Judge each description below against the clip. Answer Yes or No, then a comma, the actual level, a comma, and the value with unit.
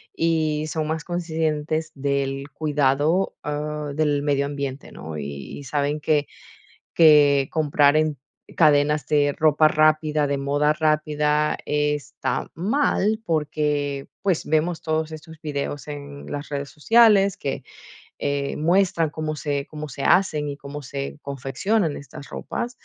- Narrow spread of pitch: Yes, narrow, 1.7 semitones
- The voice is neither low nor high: Yes, medium, 150 Hz